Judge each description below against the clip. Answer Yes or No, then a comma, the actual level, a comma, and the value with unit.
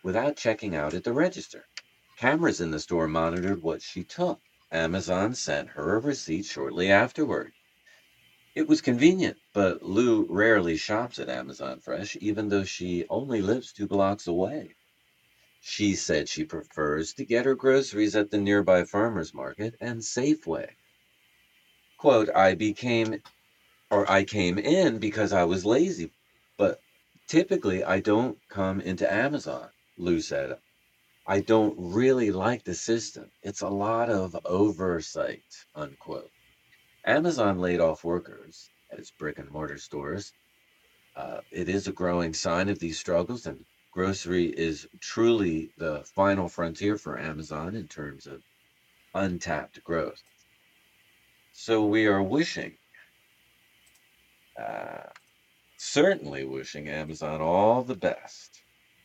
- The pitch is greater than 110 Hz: No, very low, 95 Hz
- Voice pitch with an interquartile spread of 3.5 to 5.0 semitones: Yes, average, 4.7 semitones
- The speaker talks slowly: Yes, slow, 130 wpm